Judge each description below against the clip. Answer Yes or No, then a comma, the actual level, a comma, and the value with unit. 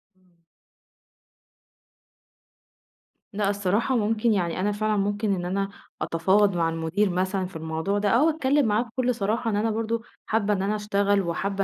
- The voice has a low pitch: No, high, 205 Hz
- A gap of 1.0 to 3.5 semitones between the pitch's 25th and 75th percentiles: Yes, narrow, 2.6 semitones